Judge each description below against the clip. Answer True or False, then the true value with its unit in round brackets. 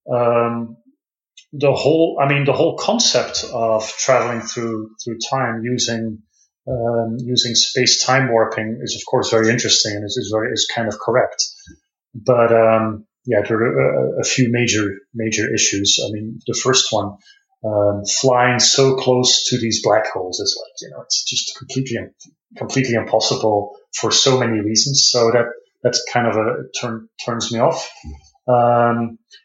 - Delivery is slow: False (165 wpm)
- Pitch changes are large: False (2.4 semitones)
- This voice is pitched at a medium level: False (115 Hz)